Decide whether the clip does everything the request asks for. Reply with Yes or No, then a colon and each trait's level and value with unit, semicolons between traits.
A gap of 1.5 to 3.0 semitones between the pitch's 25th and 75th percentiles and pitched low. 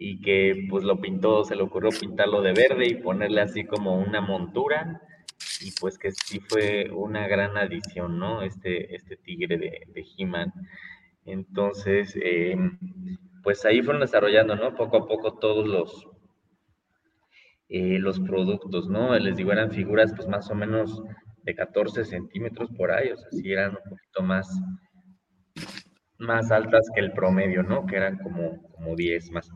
Yes: narrow, 2.5 semitones; low, 100 Hz